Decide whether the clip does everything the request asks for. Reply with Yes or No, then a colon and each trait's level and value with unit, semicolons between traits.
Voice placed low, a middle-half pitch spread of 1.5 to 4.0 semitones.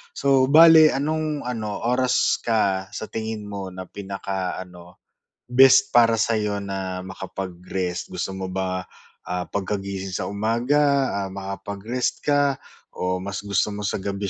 No: low, 100 Hz; average, 4.4 semitones